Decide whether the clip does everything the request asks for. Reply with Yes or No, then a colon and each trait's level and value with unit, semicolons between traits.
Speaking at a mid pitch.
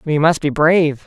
Yes: medium, 155 Hz